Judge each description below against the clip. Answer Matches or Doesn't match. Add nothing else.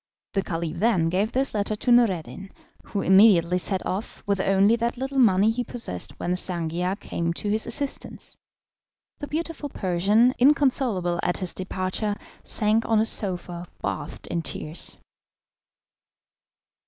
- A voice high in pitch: Matches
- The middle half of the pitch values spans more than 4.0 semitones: Matches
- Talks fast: Doesn't match